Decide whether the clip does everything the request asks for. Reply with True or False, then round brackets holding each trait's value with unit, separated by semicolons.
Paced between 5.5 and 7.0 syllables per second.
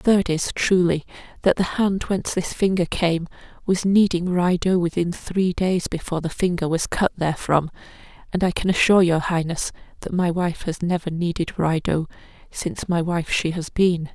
False (5.0 syllables/s)